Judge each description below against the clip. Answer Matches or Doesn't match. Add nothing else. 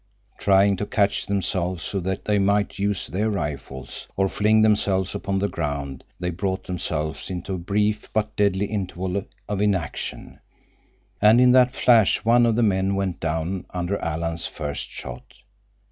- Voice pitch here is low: Matches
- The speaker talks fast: Doesn't match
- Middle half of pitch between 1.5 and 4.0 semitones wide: Matches